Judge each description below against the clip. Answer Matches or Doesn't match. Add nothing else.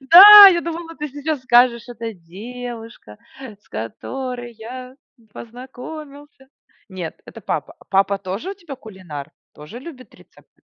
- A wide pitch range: Matches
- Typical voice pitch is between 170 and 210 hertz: Doesn't match